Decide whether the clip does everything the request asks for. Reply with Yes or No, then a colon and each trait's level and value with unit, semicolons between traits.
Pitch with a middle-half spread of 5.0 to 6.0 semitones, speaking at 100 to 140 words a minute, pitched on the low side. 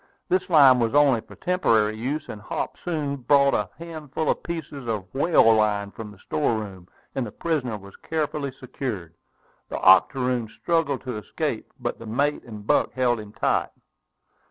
No: wide, 5.4 semitones; average, 170 wpm; low, 125 Hz